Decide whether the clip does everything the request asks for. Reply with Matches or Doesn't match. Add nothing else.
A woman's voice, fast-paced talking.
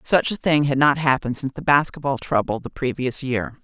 Matches